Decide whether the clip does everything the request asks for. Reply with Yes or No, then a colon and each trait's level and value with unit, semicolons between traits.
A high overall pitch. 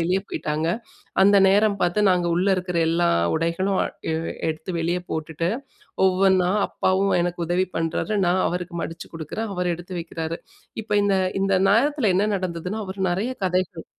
No: medium, 180 Hz